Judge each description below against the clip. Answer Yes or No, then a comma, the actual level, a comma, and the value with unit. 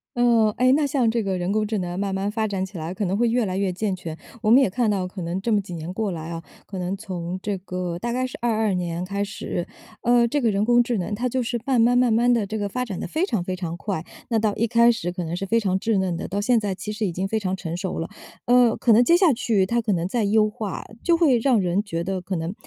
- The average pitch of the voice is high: Yes, high, 205 Hz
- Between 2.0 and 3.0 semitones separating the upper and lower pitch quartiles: No, average, 4.2 semitones